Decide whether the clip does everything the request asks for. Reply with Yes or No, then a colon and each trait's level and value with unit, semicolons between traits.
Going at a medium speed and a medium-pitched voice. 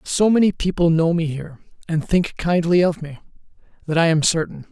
Yes: average, 190 wpm; medium, 165 Hz